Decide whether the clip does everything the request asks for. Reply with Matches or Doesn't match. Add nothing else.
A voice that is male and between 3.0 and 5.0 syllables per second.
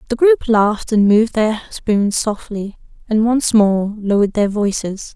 Doesn't match